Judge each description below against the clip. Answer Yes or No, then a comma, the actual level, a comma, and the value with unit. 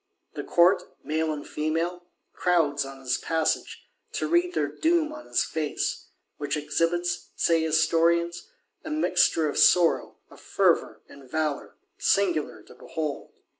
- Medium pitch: Yes, medium, 165 Hz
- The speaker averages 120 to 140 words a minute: Yes, slow, 135 wpm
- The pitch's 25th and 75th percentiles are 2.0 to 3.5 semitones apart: Yes, narrow, 2.6 semitones